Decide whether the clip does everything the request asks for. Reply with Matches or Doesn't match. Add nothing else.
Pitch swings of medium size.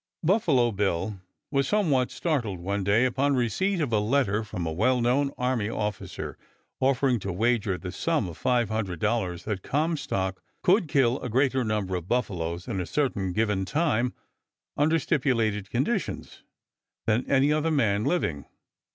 Doesn't match